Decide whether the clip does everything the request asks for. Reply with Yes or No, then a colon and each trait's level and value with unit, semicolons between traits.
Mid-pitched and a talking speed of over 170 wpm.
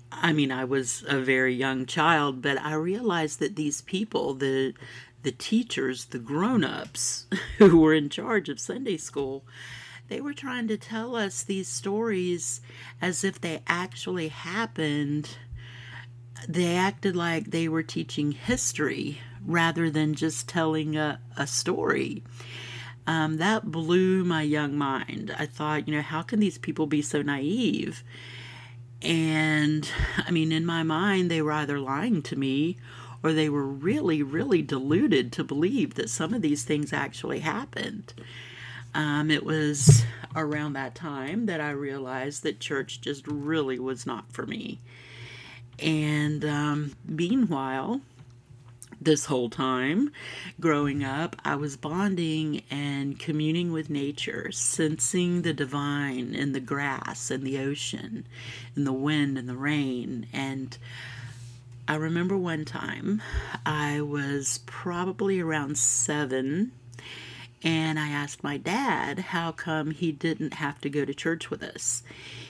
No: medium, 145 Hz; average, 140 wpm